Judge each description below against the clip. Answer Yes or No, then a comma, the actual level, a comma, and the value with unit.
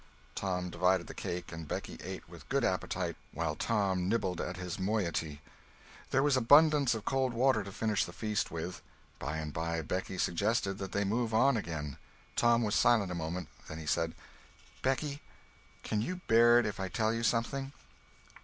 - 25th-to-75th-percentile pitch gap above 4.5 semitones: Yes, average, 5.2 semitones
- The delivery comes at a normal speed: Yes, average, 180 wpm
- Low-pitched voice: Yes, low, 100 Hz